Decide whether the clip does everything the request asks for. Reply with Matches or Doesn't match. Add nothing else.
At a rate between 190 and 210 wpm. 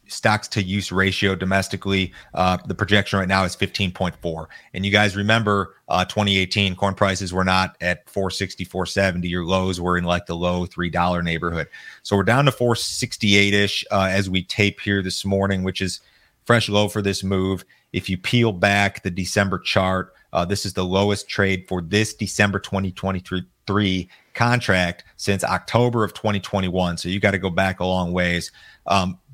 Matches